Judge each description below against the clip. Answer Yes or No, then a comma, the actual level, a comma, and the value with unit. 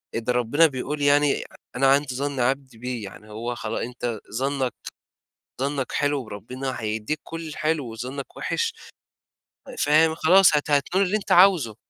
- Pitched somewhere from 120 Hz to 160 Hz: Yes, low, 135 Hz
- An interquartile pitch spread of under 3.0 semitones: No, average, 3.7 semitones